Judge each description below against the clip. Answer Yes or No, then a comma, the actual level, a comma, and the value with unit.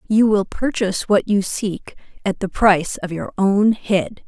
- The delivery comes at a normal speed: Yes, average, 185 wpm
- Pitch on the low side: No, high, 200 Hz